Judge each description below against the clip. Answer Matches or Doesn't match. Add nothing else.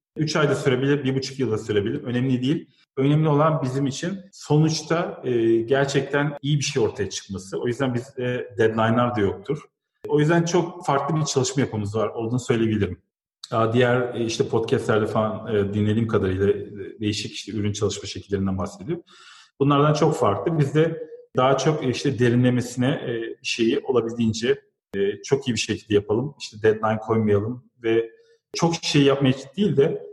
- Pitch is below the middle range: Matches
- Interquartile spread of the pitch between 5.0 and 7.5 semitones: Matches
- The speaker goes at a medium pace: Doesn't match